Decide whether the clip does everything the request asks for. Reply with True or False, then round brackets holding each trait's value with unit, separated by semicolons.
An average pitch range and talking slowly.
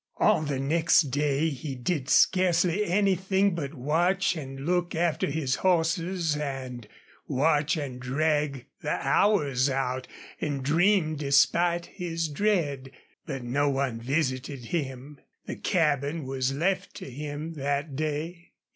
True (4.0 semitones; 130 wpm)